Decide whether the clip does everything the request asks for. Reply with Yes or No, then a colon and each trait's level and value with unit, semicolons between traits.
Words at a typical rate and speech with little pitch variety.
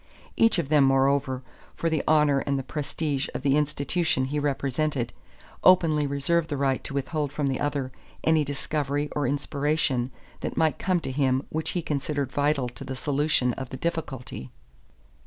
Yes: average, 165 wpm; narrow, 2.2 semitones